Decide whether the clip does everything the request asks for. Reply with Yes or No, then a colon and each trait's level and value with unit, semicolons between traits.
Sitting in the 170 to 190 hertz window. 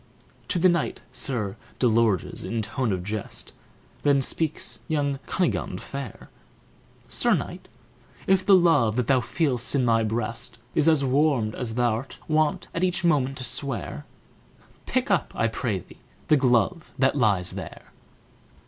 No: low, 130 Hz